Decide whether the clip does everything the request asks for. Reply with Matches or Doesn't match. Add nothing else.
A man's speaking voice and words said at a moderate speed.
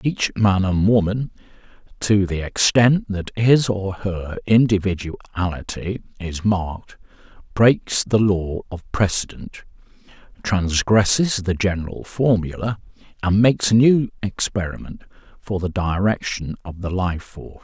Doesn't match